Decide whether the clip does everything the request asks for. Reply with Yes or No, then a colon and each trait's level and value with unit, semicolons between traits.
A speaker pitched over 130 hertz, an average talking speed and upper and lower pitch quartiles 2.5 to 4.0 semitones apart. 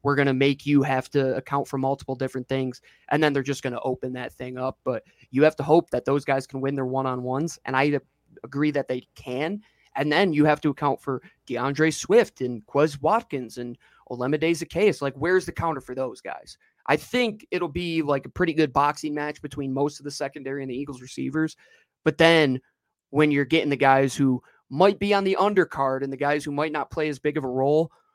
No: medium, 140 Hz; fast, 230 wpm; average, 2.8 semitones